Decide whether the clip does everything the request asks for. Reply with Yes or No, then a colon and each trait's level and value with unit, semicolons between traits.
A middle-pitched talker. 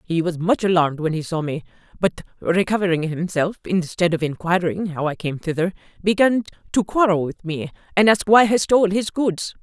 Yes: medium, 180 Hz